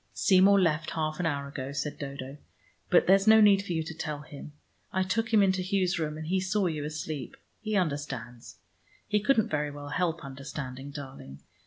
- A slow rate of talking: No, average, 190 wpm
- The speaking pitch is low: No, medium, 155 Hz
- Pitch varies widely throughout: No, average, 4.7 semitones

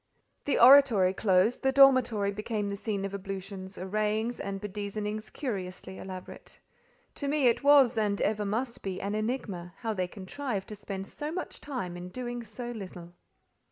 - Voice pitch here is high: Yes, high, 210 Hz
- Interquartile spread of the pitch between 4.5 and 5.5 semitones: No, average, 3.9 semitones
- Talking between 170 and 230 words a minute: No, average, 160 wpm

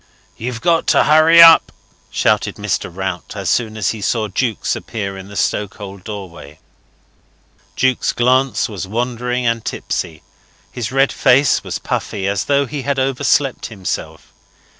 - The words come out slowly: No, average, 145 wpm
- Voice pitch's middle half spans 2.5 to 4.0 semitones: No, average, 4.8 semitones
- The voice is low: Yes, low, 115 Hz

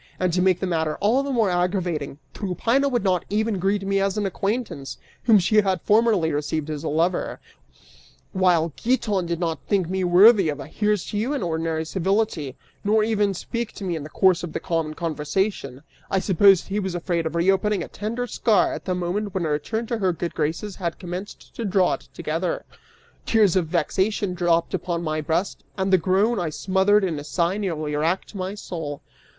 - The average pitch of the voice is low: No, medium, 185 Hz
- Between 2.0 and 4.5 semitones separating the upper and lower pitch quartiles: Yes, average, 3.7 semitones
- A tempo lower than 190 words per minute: No, average, 200 wpm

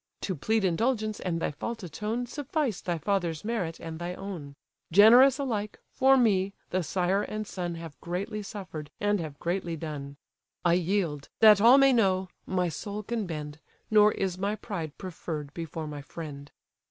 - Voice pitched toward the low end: No, medium, 185 Hz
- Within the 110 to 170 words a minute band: Yes, average, 165 wpm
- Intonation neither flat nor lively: Yes, average, 4.5 semitones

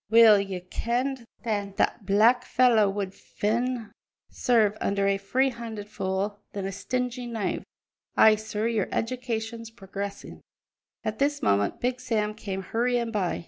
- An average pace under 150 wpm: Yes, average, 140 wpm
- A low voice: No, high, 220 Hz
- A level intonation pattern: No, average, 3.1 semitones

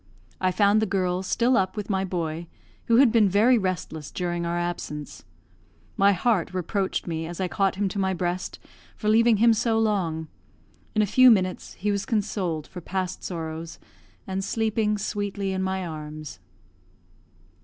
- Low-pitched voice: No, high, 190 Hz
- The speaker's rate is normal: Yes, average, 165 wpm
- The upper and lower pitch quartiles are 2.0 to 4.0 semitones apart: Yes, average, 3.4 semitones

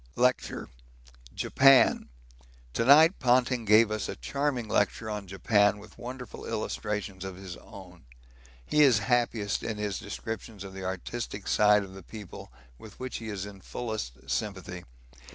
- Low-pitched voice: Yes, low, 105 Hz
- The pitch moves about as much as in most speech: Yes, average, 3.8 semitones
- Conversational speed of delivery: Yes, average, 150 wpm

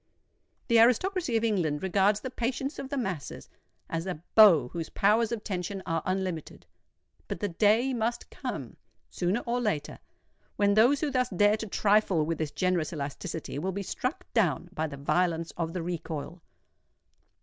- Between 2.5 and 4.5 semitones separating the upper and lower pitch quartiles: No, wide, 5.6 semitones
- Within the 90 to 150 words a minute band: No, average, 165 wpm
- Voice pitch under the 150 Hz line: No, high, 195 Hz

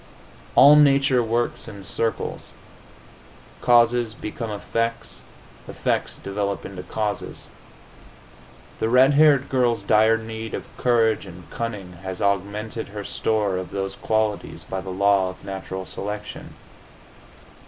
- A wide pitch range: No, average, 2.9 semitones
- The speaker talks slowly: Yes, slow, 120 wpm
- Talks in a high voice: No, low, 110 Hz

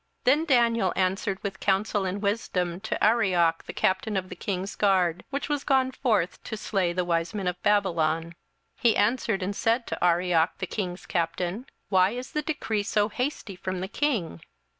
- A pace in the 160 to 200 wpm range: Yes, average, 185 wpm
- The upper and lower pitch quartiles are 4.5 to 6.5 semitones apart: No, average, 3.9 semitones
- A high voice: Yes, high, 195 Hz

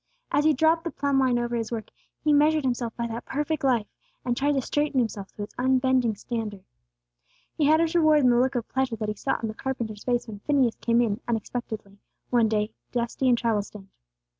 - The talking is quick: Yes, fast, 215 wpm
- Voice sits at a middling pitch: No, high, 245 Hz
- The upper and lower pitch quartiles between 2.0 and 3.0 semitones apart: No, average, 3.7 semitones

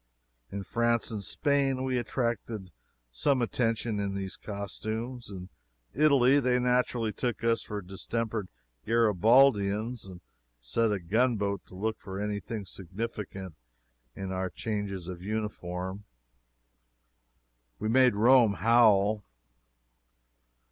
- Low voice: Yes, low, 110 Hz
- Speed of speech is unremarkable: No, slow, 115 wpm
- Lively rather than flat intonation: No, average, 3.4 semitones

